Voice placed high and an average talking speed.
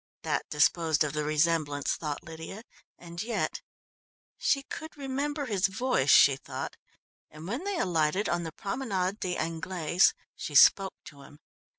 No: medium, 175 Hz; average, 150 wpm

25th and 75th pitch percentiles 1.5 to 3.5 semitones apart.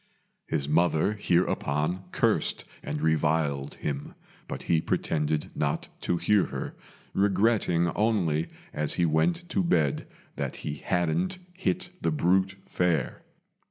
No: average, 4.3 semitones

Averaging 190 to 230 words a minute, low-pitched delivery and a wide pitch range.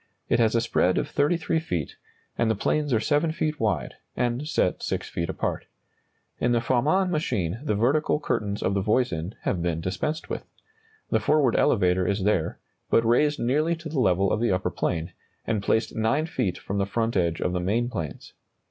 Yes: average, 195 wpm; low, 115 Hz; wide, 7.7 semitones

